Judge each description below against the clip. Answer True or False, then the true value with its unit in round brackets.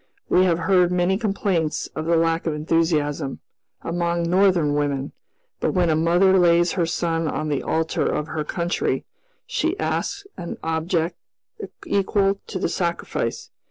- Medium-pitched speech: True (170 Hz)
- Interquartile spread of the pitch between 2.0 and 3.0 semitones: True (2.5 semitones)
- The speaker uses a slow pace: False (150 wpm)